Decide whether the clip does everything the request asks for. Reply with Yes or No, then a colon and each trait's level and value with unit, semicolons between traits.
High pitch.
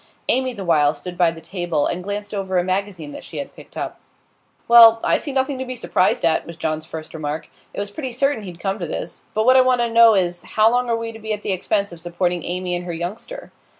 Yes: high, 195 Hz